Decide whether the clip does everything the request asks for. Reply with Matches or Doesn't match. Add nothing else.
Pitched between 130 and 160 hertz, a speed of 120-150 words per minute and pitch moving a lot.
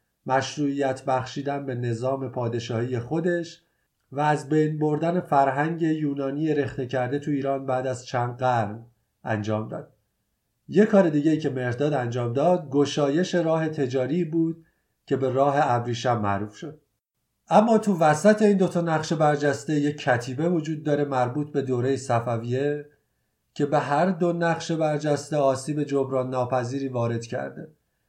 Doesn't match